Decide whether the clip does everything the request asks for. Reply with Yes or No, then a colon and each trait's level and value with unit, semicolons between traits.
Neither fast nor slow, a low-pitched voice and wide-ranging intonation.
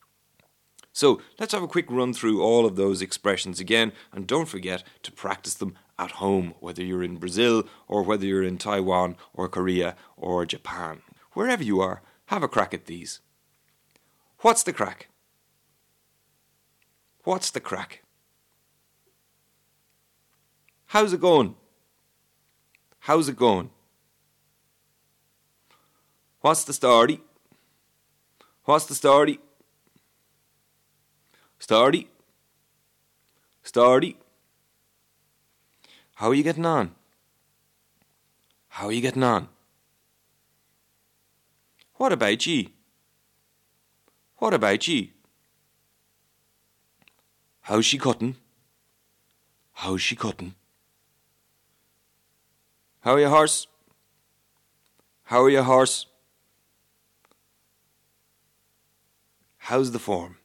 No: slow, 95 wpm; low, 115 Hz; wide, 6.3 semitones